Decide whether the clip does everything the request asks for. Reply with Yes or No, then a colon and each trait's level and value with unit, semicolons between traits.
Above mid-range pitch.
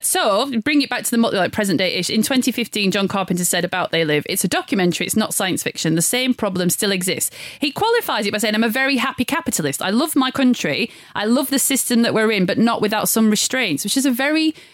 Yes: high, 220 Hz